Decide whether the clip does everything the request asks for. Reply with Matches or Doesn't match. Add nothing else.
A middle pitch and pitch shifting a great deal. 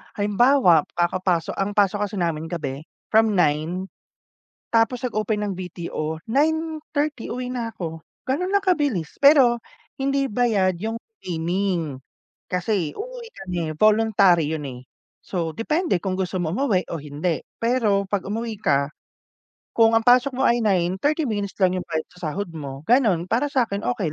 Doesn't match